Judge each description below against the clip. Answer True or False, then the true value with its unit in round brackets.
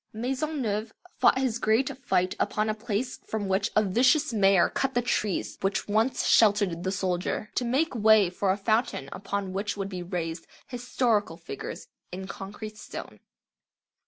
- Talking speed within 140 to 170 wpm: True (160 wpm)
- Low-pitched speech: False (210 Hz)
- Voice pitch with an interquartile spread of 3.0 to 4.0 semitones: True (3.7 semitones)